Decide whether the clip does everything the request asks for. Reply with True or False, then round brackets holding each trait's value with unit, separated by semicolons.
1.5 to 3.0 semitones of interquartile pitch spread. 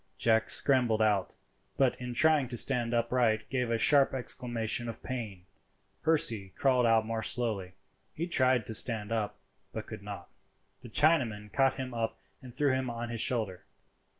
True (2.7 semitones)